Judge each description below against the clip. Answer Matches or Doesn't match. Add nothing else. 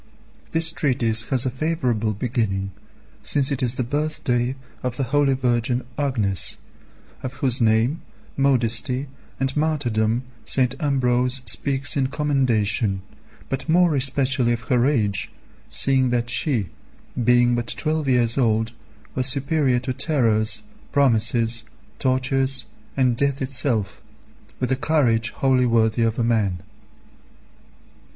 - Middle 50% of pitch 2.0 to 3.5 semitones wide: Matches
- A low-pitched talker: Matches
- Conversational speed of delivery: Doesn't match